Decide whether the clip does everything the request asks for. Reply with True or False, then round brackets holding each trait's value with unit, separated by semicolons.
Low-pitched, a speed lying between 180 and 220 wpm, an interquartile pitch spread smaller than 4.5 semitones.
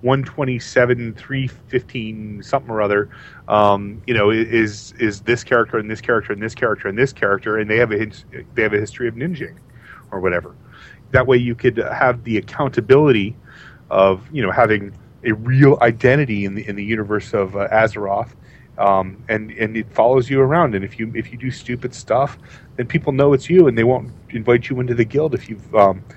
True (120 Hz; 205 wpm; 3.3 semitones)